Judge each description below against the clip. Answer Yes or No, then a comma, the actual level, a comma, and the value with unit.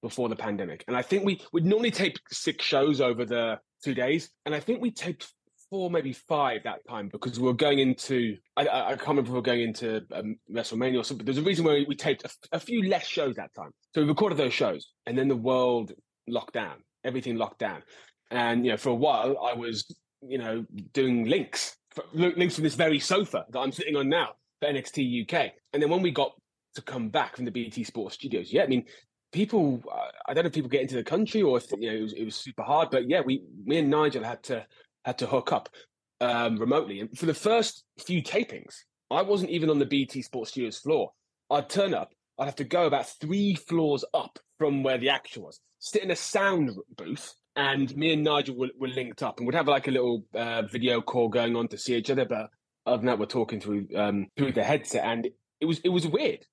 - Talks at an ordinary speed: No, fast, 240 wpm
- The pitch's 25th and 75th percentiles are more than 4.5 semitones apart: Yes, average, 5.2 semitones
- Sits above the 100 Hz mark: Yes, low, 135 Hz